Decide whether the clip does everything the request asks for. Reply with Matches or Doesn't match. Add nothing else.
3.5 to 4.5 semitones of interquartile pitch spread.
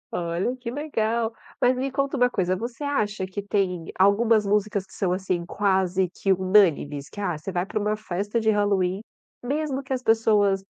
Matches